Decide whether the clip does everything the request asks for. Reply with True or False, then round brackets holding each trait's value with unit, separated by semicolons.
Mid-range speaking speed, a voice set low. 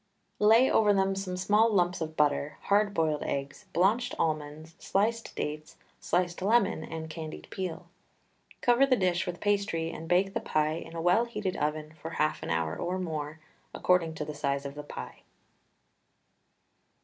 False (165 wpm; 175 Hz)